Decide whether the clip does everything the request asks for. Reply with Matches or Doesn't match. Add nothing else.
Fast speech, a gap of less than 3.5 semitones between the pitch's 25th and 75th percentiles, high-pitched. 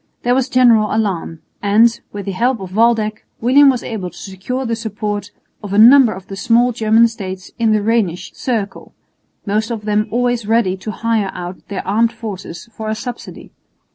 Doesn't match